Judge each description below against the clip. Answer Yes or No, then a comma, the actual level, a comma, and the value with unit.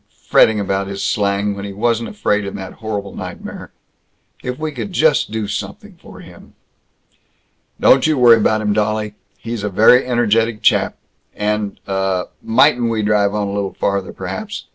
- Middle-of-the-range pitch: No, low, 105 Hz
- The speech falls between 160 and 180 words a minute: Yes, average, 165 wpm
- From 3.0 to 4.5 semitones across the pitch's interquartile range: No, narrow, 2.5 semitones